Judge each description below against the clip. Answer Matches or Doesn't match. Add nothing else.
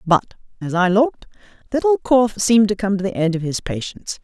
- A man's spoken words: Doesn't match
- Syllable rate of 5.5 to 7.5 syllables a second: Matches